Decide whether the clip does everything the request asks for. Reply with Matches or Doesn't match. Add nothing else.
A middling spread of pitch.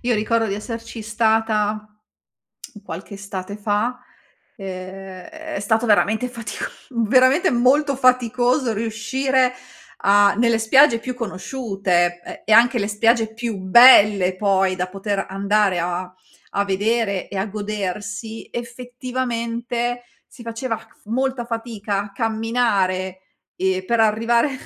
Matches